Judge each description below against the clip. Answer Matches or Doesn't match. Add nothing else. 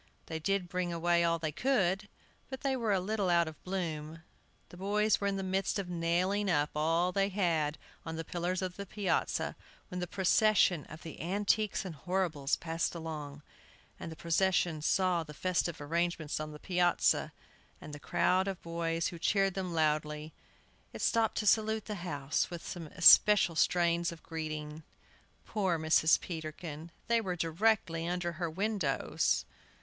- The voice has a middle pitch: Matches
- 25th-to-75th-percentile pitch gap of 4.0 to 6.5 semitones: Doesn't match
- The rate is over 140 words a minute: Matches